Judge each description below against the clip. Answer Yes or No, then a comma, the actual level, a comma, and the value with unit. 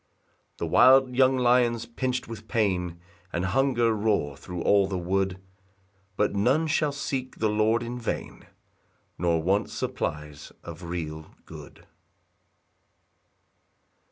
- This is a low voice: Yes, low, 105 Hz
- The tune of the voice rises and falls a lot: Yes, wide, 5.8 semitones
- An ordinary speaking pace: No, slow, 125 wpm